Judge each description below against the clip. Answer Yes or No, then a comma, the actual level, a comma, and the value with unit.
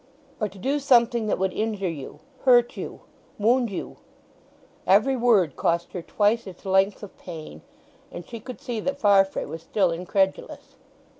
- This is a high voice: Yes, high, 205 Hz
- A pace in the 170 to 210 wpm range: No, average, 145 wpm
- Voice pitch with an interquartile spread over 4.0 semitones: Yes, average, 4.4 semitones